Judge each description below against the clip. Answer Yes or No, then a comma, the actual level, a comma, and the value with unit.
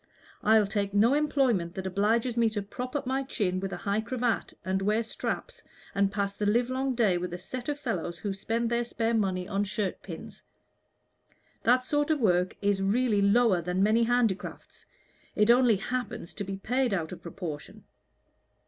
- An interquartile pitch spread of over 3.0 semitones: Yes, average, 4.0 semitones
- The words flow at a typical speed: Yes, average, 180 wpm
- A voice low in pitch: No, high, 215 Hz